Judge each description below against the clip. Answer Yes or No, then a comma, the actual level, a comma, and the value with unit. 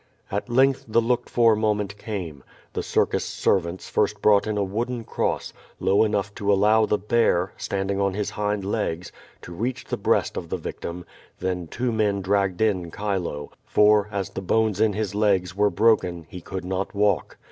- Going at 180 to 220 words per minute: Yes, average, 190 wpm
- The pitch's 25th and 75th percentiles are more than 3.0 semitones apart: No, narrow, 2.5 semitones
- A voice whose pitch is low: Yes, low, 100 Hz